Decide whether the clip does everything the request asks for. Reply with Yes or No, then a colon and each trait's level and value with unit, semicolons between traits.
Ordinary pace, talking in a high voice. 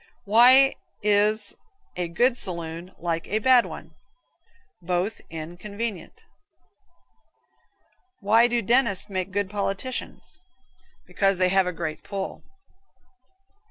No: slow, 105 wpm; high, 200 Hz